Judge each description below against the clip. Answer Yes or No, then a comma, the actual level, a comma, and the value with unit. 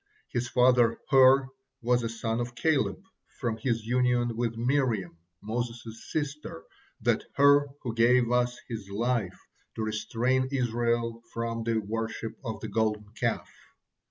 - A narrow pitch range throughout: Yes, narrow, 1.9 semitones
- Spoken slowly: Yes, slow, 130 wpm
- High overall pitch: No, low, 115 Hz